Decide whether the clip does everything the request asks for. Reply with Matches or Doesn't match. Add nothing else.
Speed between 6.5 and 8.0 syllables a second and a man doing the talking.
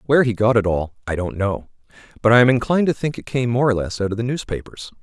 Matches